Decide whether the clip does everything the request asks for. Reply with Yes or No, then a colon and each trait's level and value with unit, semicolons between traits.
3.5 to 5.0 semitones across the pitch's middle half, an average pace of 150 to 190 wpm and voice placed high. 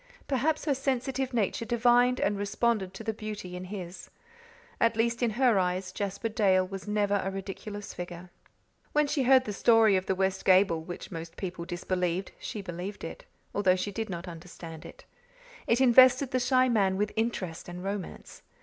Yes: average, 4.4 semitones; average, 175 wpm; high, 205 Hz